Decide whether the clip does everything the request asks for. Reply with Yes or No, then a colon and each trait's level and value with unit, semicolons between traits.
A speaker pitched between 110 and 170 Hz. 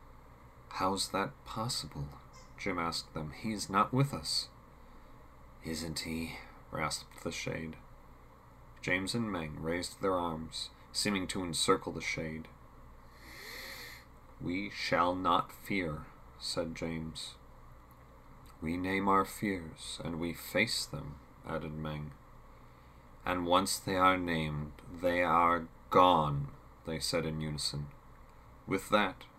No: very low, 80 Hz